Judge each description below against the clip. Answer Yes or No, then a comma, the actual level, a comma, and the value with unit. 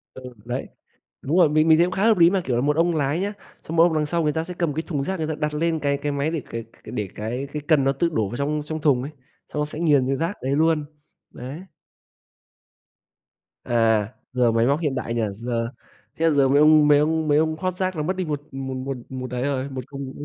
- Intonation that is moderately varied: Yes, average, 3.5 semitones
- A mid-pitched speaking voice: Yes, medium, 150 Hz